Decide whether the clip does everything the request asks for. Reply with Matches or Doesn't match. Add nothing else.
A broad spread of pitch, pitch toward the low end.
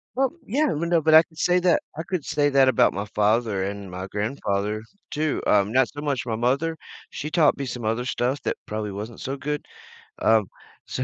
Matches